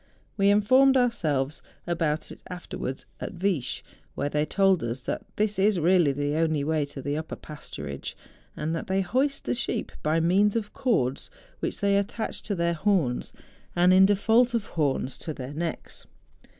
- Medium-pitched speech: Yes, medium, 175 Hz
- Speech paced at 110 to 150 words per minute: No, average, 165 wpm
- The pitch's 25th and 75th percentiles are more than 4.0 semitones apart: Yes, wide, 5.4 semitones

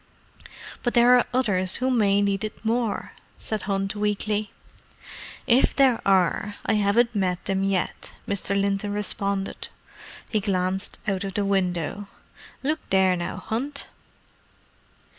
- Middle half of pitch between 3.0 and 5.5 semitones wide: No, narrow, 2.4 semitones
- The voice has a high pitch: Yes, high, 200 Hz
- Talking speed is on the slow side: Yes, slow, 130 wpm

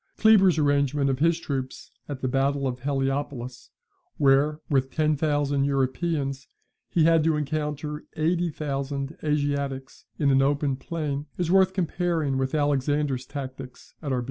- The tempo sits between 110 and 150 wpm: Yes, average, 145 wpm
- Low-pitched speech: No, medium, 145 Hz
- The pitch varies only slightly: Yes, narrow, 2.3 semitones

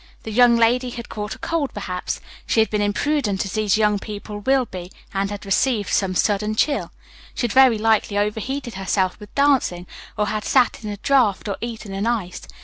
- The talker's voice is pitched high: Yes, high, 215 Hz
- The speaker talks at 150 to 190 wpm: No, average, 200 wpm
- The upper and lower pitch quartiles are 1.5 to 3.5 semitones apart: Yes, average, 3.0 semitones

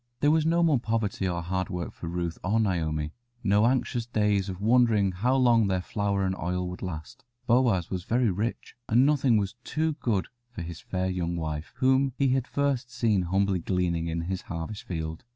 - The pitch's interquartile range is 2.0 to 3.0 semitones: No, average, 5.3 semitones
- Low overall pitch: Yes, low, 100 Hz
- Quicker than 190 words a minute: Yes, average, 200 wpm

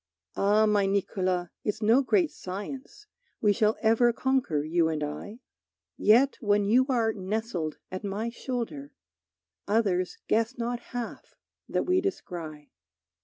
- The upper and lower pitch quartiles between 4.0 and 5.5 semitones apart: Yes, average, 4.6 semitones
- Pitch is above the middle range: Yes, high, 215 Hz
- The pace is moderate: No, slow, 130 wpm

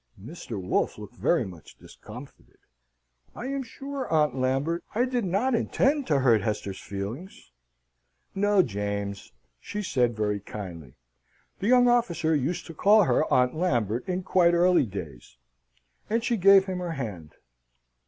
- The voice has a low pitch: No, medium, 160 Hz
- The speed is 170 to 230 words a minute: No, average, 145 wpm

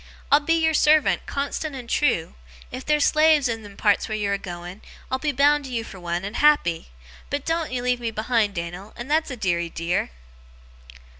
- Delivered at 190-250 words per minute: Yes, average, 200 wpm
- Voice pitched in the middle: No, high, 245 Hz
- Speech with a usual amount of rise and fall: No, wide, 6.9 semitones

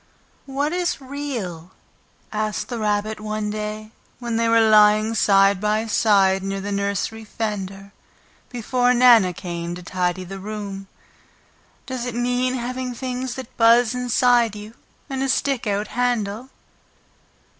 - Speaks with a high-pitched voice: Yes, high, 215 Hz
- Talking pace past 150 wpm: No, slow, 135 wpm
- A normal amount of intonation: Yes, average, 3.6 semitones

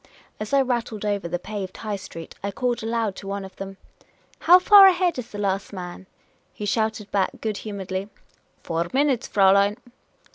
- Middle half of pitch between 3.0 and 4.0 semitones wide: Yes, average, 3.3 semitones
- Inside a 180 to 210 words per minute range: Yes, average, 185 wpm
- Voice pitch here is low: No, high, 205 Hz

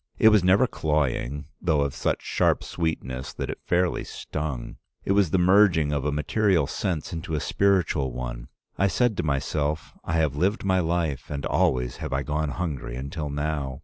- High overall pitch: No, very low, 75 Hz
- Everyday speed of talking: Yes, average, 180 wpm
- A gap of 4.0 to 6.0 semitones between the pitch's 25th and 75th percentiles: Yes, average, 4.3 semitones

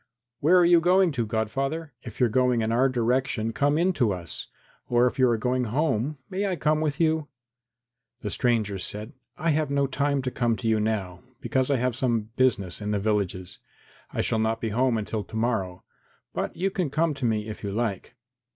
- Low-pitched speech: Yes, low, 125 Hz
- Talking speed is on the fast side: Yes, fast, 215 wpm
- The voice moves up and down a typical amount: Yes, average, 4.8 semitones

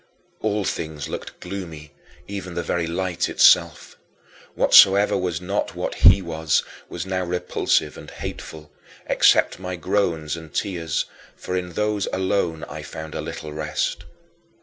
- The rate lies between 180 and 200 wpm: No, average, 140 wpm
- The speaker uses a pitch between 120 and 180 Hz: No, very low, 90 Hz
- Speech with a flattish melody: No, average, 3.1 semitones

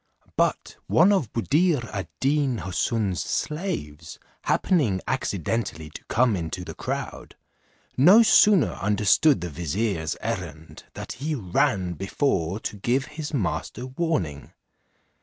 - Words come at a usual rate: No, slow, 120 wpm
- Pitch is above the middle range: No, low, 115 Hz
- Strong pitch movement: Yes, wide, 8.7 semitones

